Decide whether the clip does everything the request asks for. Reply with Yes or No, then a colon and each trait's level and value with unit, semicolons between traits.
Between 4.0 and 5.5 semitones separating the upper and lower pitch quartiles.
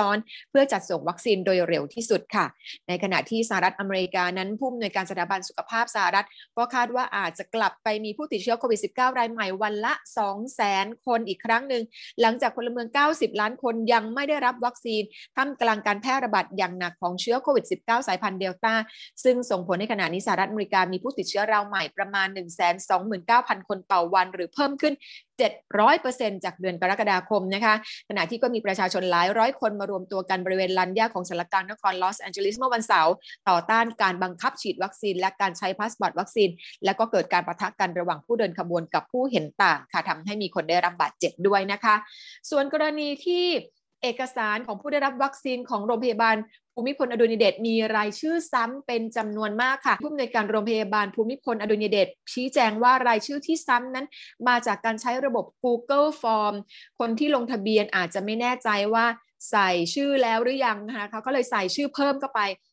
Yes: average, 4.3 semitones